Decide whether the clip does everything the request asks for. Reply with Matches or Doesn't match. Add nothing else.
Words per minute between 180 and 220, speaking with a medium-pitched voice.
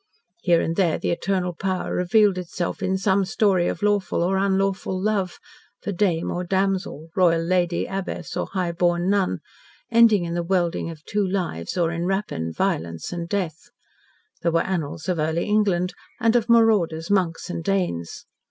Doesn't match